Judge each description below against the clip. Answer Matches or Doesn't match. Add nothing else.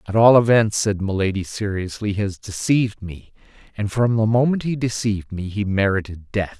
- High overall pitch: Doesn't match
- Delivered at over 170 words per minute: Matches